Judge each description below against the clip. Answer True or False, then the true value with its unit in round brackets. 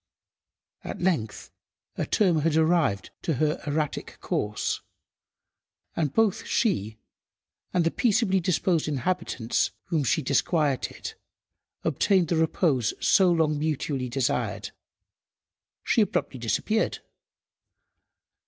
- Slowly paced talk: True (100 wpm)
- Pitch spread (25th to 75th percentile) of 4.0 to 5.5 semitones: True (4.9 semitones)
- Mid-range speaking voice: True (155 Hz)